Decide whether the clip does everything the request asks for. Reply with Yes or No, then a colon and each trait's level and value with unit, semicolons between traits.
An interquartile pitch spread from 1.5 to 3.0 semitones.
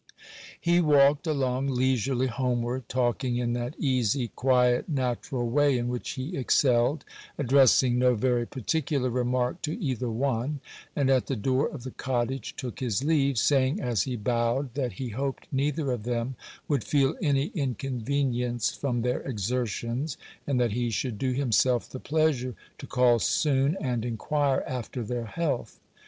Yes: narrow, 2.4 semitones